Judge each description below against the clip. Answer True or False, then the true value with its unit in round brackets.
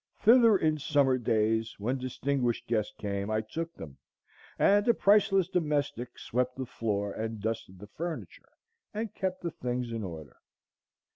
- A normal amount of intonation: False (7.2 semitones)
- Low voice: True (125 Hz)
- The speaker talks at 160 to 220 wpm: False (150 wpm)